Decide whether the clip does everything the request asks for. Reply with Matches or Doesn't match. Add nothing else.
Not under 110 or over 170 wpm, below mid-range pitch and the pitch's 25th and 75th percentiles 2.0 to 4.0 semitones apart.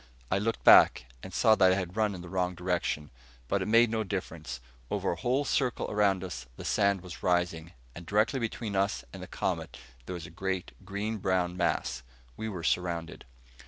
Doesn't match